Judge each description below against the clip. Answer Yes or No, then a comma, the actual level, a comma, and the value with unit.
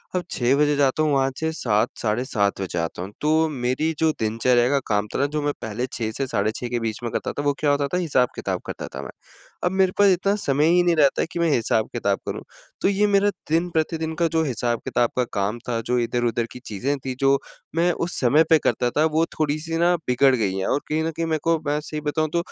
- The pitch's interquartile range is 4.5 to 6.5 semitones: Yes, average, 5.1 semitones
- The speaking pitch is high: No, medium, 140 Hz